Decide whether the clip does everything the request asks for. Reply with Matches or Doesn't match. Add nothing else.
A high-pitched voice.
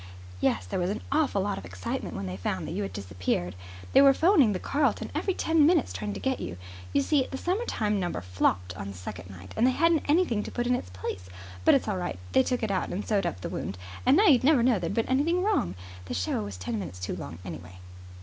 Matches